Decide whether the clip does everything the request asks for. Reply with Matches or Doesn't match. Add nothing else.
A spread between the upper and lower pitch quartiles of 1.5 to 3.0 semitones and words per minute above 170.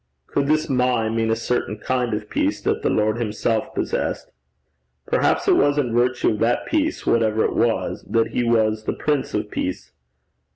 Matches